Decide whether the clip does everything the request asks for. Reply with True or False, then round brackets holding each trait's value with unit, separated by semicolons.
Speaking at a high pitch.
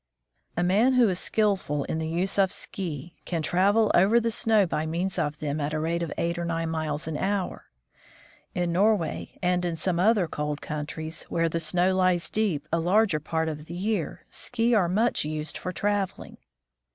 False (175 Hz)